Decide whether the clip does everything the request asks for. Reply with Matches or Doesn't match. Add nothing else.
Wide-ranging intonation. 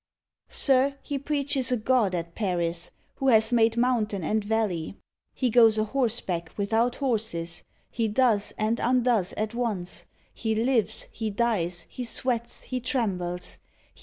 Doesn't match